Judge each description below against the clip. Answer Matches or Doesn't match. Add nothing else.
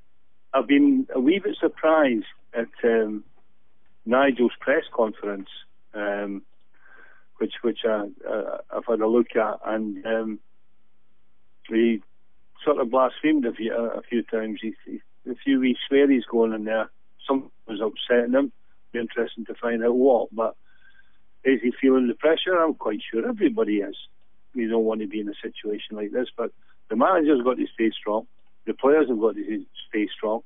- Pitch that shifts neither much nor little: Matches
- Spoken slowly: Doesn't match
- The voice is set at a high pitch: Doesn't match